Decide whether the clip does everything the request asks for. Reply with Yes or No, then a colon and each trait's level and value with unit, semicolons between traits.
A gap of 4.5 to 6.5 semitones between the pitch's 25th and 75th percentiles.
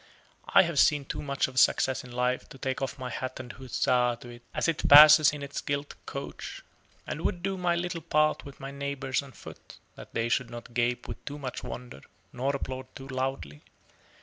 No: average, 2.7 semitones